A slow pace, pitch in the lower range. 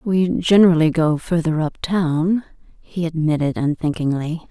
No: slow, 120 wpm; medium, 165 Hz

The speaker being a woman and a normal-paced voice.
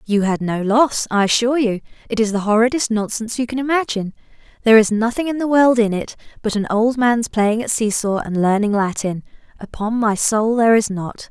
No: female; fast, 210 wpm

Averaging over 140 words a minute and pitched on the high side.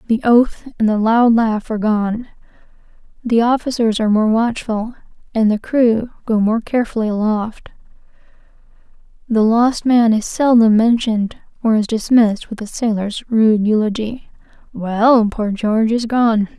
No: slow, 135 wpm; high, 225 Hz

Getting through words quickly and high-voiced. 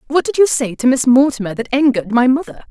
Yes: fast, 245 wpm; very high, 260 Hz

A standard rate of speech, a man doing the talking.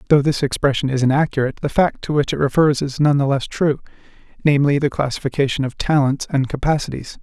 Yes: average, 190 wpm; male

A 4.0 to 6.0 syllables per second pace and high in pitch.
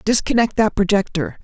Yes: 5.3 syllables/s; high, 200 Hz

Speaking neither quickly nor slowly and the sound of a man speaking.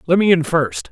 No: fast, 265 wpm; male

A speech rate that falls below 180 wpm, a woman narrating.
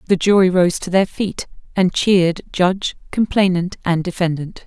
Yes: average, 155 wpm; female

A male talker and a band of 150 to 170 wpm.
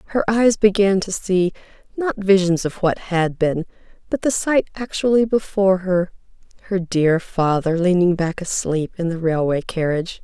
No: female; average, 160 wpm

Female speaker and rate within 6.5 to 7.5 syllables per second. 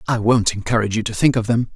No: male; 7.0 syllables/s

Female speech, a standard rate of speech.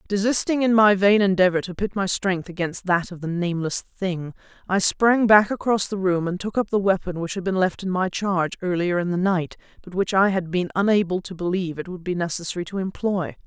No: female; fast, 225 wpm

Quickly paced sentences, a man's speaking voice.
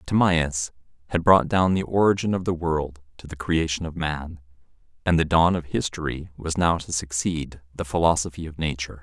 No: average, 180 wpm; male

